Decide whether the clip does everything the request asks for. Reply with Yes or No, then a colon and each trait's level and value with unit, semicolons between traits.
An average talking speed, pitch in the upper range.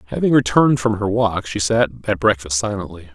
No: average, 190 wpm; very low, 95 Hz